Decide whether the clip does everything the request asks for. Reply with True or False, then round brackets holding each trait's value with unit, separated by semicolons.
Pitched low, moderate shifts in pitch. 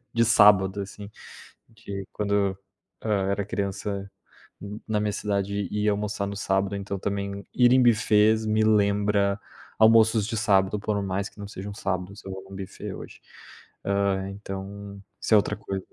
False (100 Hz; 1.3 semitones)